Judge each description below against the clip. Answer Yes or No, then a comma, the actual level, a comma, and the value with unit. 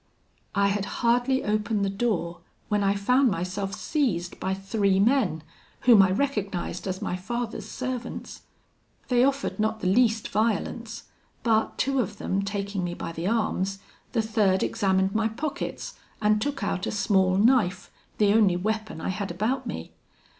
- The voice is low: No, high, 210 Hz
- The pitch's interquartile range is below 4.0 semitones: Yes, average, 3.5 semitones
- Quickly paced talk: No, average, 160 wpm